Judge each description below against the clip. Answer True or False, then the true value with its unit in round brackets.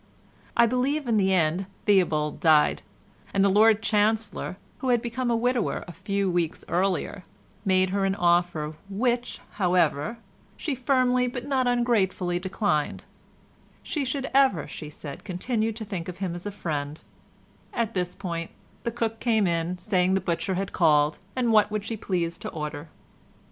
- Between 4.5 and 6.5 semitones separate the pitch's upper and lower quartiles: True (5.0 semitones)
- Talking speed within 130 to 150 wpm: False (160 wpm)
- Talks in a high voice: True (195 Hz)